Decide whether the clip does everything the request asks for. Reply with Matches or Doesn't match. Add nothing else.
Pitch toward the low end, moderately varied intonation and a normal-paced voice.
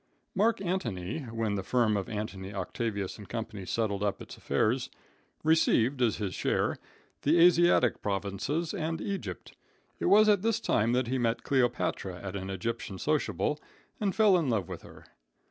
Doesn't match